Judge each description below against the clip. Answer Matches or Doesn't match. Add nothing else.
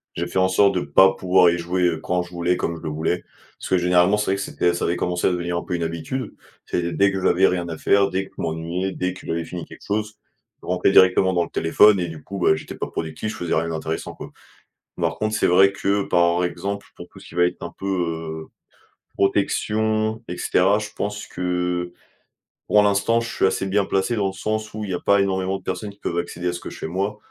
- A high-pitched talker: Doesn't match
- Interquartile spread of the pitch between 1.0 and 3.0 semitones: Matches